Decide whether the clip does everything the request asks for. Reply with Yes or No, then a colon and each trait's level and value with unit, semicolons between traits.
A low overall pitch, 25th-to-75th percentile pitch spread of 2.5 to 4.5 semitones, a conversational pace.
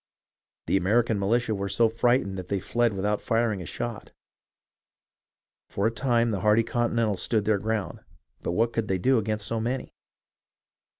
Yes: low, 110 Hz; average, 2.8 semitones; average, 165 wpm